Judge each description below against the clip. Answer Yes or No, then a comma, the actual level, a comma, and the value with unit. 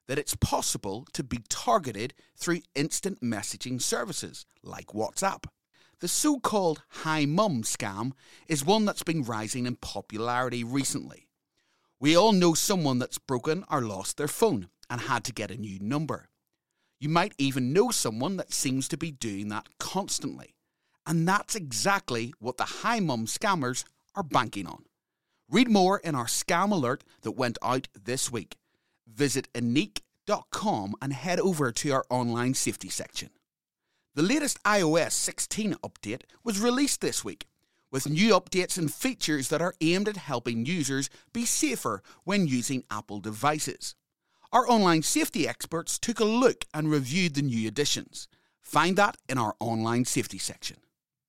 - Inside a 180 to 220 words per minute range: No, average, 155 wpm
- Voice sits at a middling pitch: Yes, medium, 145 Hz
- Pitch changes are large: Yes, wide, 7.1 semitones